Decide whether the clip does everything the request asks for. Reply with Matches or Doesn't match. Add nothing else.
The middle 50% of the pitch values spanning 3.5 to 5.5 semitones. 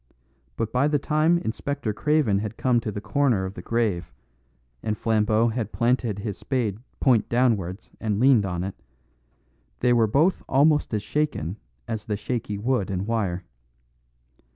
Matches